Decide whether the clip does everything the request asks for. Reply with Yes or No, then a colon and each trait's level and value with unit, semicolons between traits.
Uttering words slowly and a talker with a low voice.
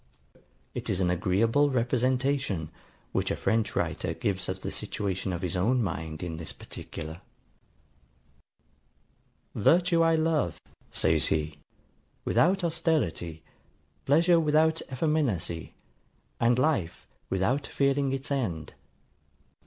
Yes: slow, 110 wpm; low, 120 Hz